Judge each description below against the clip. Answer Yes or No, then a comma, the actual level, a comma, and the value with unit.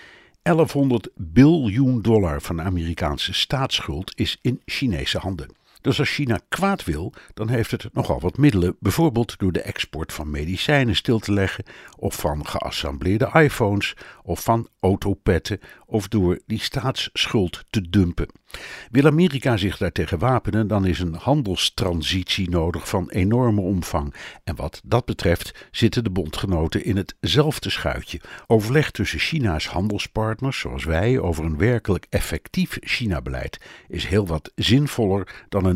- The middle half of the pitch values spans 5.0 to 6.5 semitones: Yes, wide, 5.4 semitones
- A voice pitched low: Yes, low, 100 Hz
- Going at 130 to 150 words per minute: Yes, average, 140 wpm